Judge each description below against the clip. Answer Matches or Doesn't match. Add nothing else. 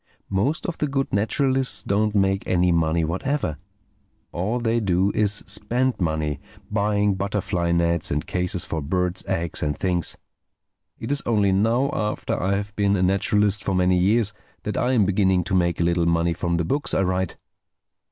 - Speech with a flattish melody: Doesn't match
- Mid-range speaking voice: Doesn't match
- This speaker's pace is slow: Doesn't match